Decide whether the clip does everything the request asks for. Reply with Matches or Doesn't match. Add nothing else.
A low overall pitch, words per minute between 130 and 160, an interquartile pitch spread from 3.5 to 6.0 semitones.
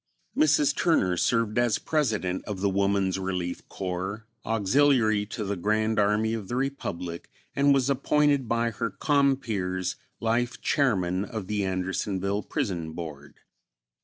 Matches